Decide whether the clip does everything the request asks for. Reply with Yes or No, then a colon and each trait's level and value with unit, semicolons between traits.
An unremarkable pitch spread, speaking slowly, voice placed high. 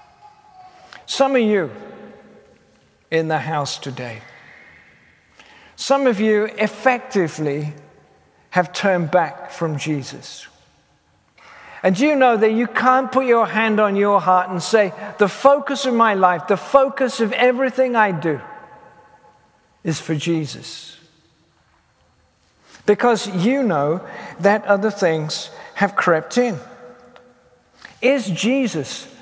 No: wide, 7.5 semitones; slow, 115 wpm; high, 200 Hz